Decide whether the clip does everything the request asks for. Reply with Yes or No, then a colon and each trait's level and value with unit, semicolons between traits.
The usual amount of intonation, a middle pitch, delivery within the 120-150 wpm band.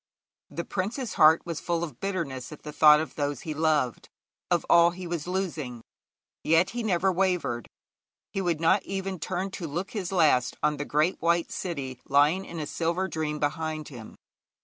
No: average, 3.5 semitones; medium, 165 Hz; average, 185 wpm